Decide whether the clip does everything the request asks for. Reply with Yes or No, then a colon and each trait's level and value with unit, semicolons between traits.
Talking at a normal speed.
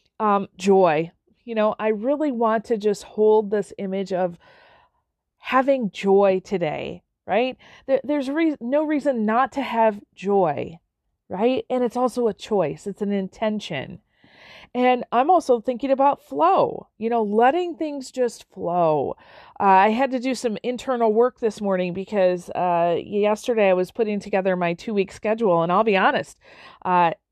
Yes: average, 160 wpm